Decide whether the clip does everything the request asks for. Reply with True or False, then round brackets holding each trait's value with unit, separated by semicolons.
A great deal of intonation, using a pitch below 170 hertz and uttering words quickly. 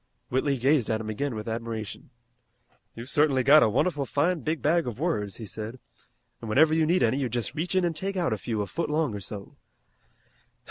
True (5.9 semitones; 135 Hz; 215 wpm)